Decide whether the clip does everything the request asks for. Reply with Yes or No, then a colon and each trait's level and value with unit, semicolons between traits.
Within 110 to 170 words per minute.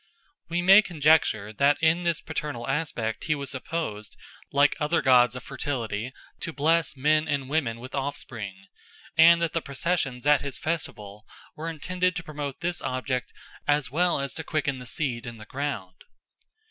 Yes: average, 165 wpm